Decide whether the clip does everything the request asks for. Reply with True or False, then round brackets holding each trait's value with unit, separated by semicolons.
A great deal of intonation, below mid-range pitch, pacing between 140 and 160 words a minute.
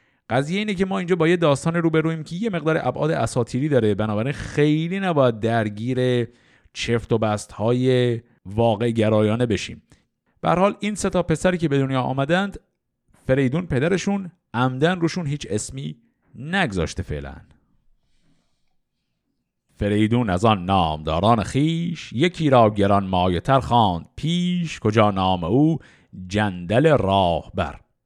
False (7.2 semitones; 125 Hz; 125 wpm)